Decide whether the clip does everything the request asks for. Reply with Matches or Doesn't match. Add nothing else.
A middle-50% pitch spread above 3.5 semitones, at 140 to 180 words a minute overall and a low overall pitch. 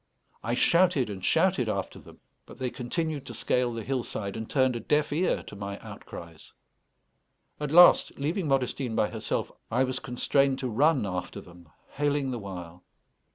Matches